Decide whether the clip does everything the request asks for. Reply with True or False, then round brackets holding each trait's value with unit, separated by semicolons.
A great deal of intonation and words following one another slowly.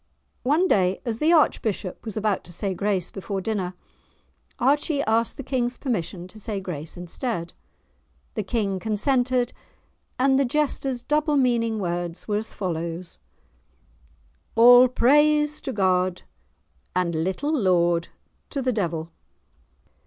True (6.0 semitones; 130 wpm)